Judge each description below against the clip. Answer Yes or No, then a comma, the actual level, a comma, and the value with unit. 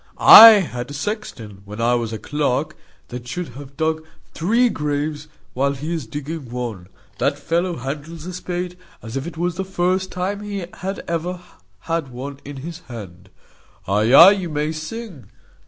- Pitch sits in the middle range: Yes, medium, 155 Hz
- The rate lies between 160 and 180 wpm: Yes, average, 170 wpm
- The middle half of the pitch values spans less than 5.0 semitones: No, wide, 5.6 semitones